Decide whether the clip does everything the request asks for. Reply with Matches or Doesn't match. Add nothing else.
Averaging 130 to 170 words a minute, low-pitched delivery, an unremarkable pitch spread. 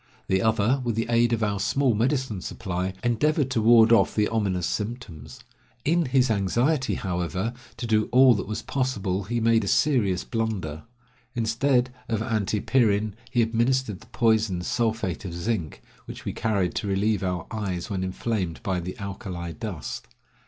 Matches